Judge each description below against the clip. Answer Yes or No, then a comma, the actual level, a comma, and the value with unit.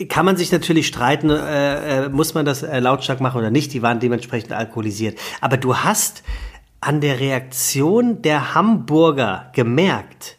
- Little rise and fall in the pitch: No, average, 4.3 semitones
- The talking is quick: No, average, 160 wpm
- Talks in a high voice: No, medium, 140 Hz